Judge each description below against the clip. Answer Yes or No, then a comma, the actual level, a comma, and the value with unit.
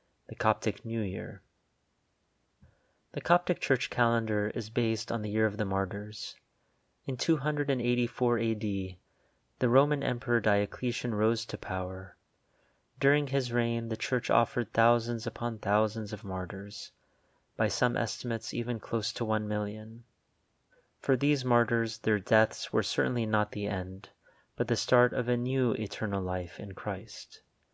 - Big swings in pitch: No, average, 2.7 semitones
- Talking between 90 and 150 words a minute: Yes, average, 140 wpm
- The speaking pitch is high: No, low, 115 Hz